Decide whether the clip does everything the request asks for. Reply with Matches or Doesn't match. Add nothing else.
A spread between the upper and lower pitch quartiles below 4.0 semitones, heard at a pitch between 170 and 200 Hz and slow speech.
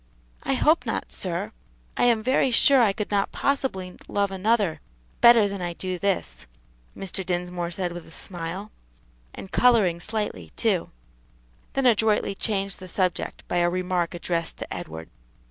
Doesn't match